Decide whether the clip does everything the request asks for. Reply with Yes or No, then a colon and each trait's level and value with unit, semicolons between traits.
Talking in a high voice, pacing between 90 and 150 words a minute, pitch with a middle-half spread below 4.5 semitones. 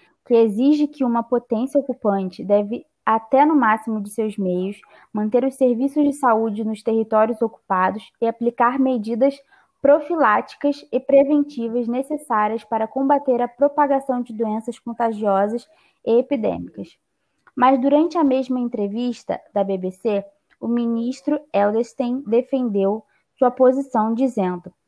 Yes: high, 240 Hz; average, 125 wpm; average, 3.6 semitones